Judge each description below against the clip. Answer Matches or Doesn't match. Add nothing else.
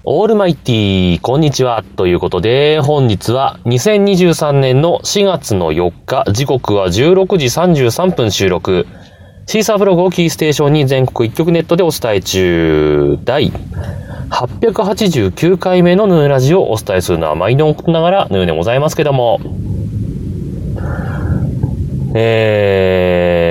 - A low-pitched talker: Matches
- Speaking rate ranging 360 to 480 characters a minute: Doesn't match